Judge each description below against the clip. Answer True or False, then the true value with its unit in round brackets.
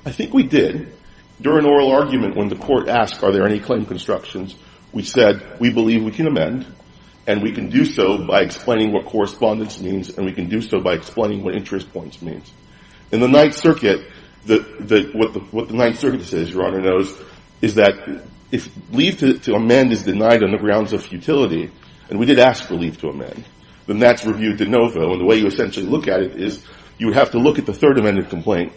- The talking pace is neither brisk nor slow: False (220 wpm)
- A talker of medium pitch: False (110 Hz)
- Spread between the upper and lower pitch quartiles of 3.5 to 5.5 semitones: True (4.0 semitones)